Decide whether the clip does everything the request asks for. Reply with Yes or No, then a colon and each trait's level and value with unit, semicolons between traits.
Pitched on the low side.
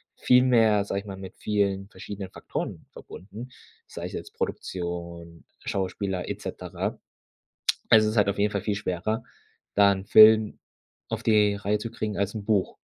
Yes: low, 100 Hz